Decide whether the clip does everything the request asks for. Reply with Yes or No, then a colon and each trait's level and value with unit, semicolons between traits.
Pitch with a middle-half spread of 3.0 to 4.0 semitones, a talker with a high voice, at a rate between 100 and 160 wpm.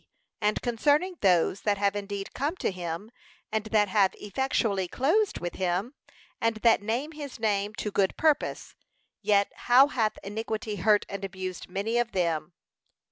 Yes: average, 3.6 semitones; high, 210 Hz; average, 155 wpm